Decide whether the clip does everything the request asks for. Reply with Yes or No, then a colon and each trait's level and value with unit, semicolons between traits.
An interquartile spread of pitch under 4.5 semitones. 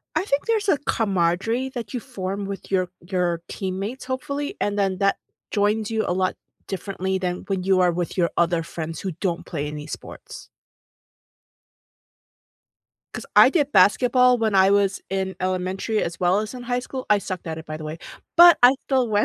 No: average, 4.9 semitones